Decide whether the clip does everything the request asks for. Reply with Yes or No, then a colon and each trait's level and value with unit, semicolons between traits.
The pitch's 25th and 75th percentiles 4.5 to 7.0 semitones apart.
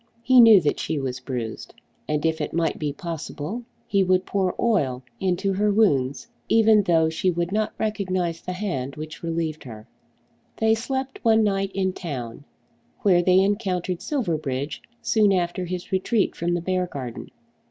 Yes: average, 4.8 semitones